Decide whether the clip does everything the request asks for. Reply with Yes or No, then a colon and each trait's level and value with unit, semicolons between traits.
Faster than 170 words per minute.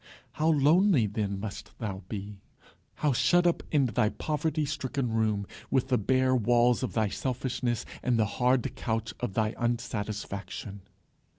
No: average, 150 wpm